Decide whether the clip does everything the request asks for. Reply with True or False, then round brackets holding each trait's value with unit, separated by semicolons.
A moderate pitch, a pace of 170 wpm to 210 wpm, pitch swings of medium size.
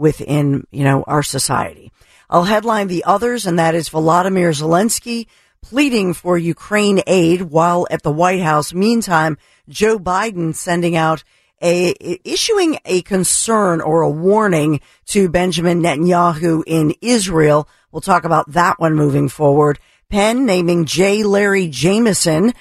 False (175 Hz; 140 wpm; 4.0 semitones)